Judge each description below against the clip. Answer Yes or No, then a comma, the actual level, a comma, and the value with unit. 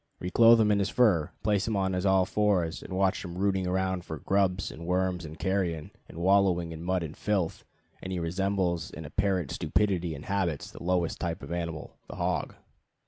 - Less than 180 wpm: No, average, 195 wpm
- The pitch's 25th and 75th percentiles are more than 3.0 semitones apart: No, narrow, 2.5 semitones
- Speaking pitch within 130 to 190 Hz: No, very low, 90 Hz